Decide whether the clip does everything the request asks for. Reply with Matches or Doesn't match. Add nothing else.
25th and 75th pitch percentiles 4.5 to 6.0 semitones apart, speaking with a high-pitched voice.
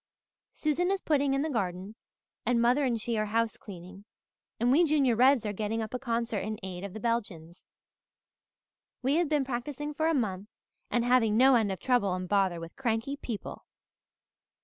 Matches